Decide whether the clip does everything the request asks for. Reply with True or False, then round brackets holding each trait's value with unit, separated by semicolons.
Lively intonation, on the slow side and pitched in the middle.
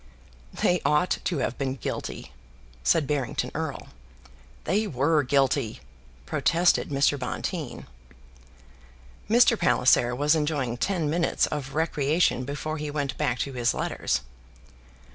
False (3.6 semitones; 120 wpm; 145 Hz)